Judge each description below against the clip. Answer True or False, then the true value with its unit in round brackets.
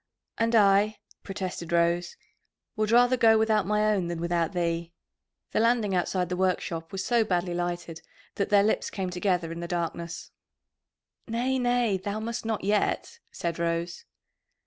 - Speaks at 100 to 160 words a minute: True (155 wpm)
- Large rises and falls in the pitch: False (4.1 semitones)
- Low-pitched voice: False (190 Hz)